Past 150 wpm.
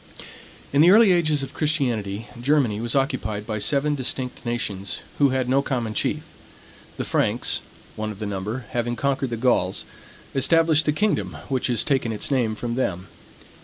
Yes: average, 165 wpm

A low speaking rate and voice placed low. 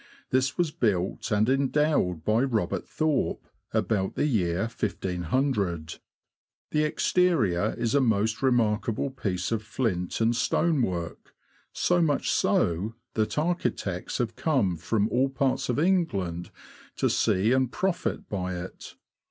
Yes: slow, 130 wpm; low, 115 Hz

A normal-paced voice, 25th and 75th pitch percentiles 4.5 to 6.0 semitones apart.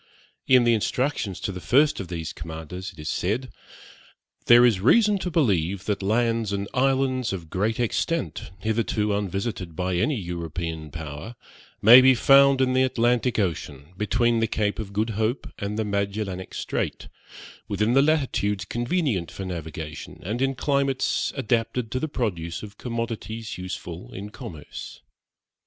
Yes: average, 150 wpm; average, 5.2 semitones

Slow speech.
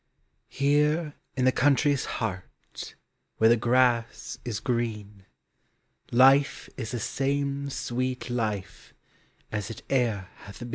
Yes: slow, 115 wpm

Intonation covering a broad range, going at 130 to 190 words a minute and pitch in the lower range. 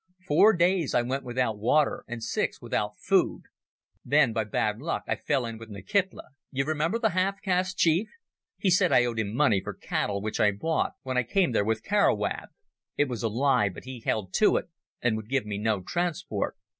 No: wide, 7.4 semitones; average, 200 wpm; low, 130 Hz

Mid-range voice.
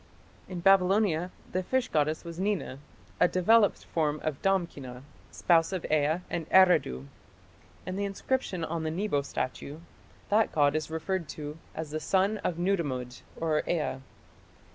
Yes: medium, 170 Hz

